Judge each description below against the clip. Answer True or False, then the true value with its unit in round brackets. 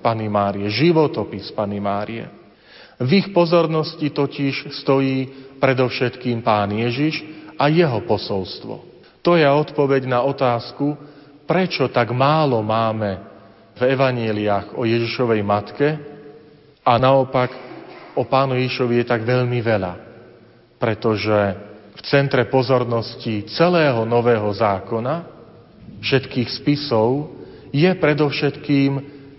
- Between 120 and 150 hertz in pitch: True (125 Hz)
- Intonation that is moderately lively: True (4.3 semitones)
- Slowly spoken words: True (100 wpm)